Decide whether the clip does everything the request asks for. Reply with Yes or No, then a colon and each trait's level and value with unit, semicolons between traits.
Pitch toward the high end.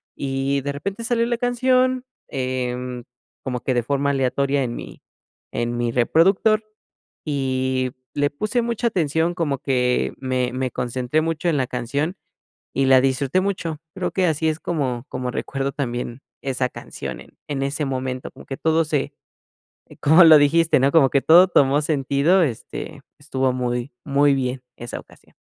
No: medium, 140 Hz